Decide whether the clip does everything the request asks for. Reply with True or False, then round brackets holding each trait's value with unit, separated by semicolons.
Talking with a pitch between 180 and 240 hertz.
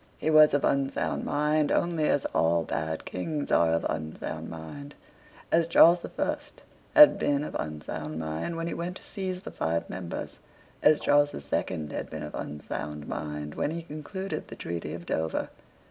False (140 Hz)